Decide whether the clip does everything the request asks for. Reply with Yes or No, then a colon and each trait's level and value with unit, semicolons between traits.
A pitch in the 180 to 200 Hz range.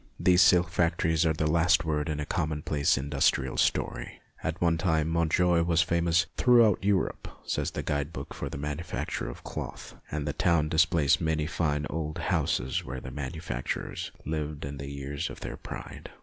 No: very low, 80 Hz